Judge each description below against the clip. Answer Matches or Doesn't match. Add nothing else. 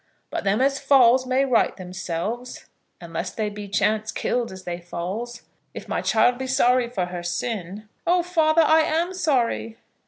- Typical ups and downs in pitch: Doesn't match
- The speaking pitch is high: Matches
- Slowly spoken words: Doesn't match